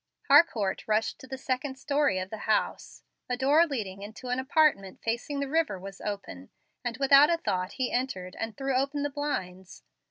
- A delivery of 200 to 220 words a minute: No, average, 185 wpm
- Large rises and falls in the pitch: Yes, wide, 6.0 semitones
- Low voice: No, very high, 255 Hz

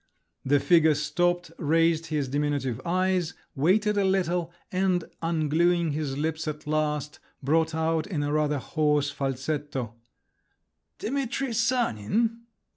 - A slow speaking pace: Yes, slow, 120 wpm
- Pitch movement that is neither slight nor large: Yes, average, 3.4 semitones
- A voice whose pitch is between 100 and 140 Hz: No, medium, 160 Hz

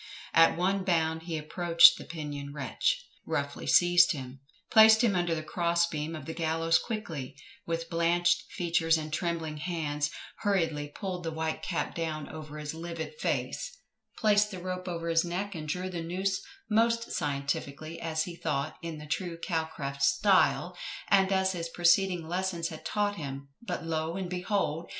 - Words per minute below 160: No, average, 165 wpm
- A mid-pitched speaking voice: Yes, medium, 165 Hz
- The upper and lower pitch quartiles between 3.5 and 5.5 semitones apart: No, average, 2.7 semitones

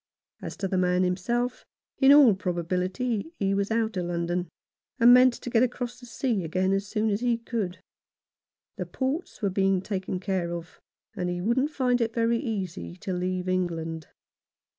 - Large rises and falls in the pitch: No, average, 4.7 semitones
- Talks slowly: No, average, 175 wpm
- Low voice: No, high, 195 Hz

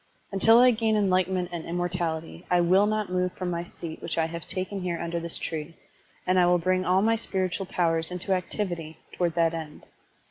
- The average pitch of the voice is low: No, medium, 180 Hz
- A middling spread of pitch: No, narrow, 2.0 semitones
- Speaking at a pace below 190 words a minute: No, average, 200 wpm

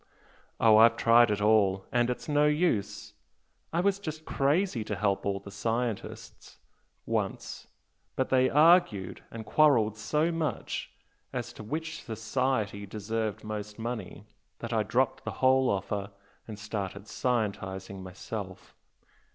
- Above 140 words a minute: No, slow, 135 wpm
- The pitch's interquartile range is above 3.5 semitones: Yes, average, 4.5 semitones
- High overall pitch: No, low, 110 Hz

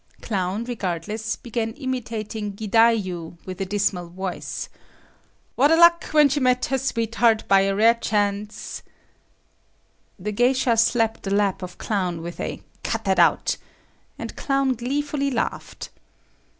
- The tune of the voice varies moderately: Yes, average, 4.2 semitones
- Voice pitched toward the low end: No, high, 220 Hz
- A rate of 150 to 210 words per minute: No, slow, 135 wpm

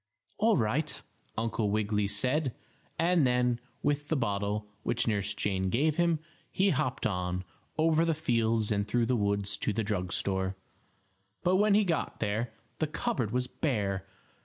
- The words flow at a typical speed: Yes, average, 160 wpm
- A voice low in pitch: Yes, low, 115 Hz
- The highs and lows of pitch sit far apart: Yes, wide, 6.9 semitones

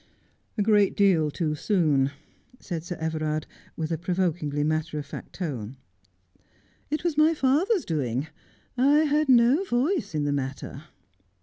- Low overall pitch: No, medium, 170 Hz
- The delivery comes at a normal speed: Yes, average, 150 wpm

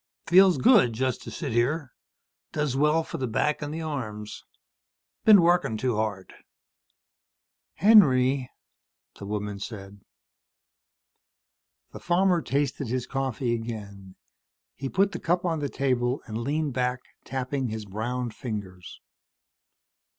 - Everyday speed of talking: No, slow, 125 wpm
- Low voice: Yes, low, 130 Hz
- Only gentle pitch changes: No, average, 5.3 semitones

